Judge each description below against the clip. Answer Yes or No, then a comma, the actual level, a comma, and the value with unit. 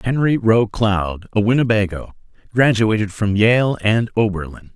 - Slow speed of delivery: Yes, slow, 125 wpm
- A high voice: No, low, 110 Hz